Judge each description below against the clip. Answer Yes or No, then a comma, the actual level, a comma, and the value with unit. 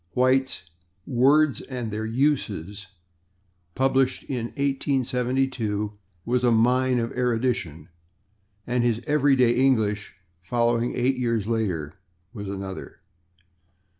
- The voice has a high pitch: No, low, 120 Hz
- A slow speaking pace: Yes, slow, 100 wpm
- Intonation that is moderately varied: Yes, average, 3.3 semitones